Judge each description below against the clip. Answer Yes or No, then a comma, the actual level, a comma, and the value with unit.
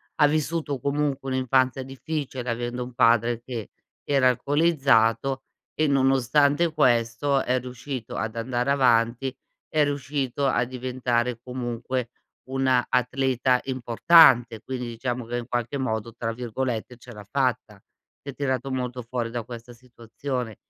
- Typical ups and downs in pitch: No, narrow, 2.3 semitones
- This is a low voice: Yes, low, 125 Hz